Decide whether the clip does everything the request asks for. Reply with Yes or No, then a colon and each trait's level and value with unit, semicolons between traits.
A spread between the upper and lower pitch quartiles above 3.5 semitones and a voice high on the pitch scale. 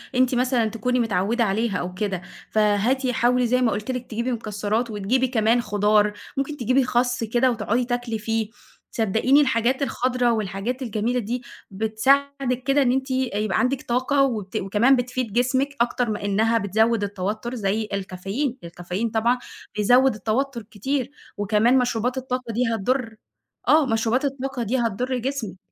No: average, 3.1 semitones; high, 235 Hz